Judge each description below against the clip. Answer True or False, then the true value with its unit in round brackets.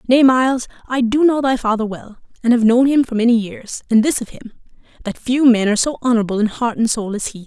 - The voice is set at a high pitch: True (235 Hz)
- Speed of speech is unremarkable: False (250 wpm)